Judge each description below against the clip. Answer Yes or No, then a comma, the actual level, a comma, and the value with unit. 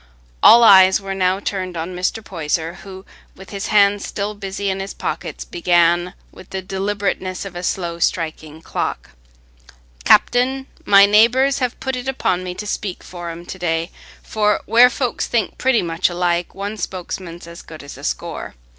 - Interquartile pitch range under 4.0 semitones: Yes, average, 3.1 semitones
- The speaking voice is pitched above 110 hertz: Yes, high, 190 Hz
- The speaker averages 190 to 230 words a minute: No, average, 170 wpm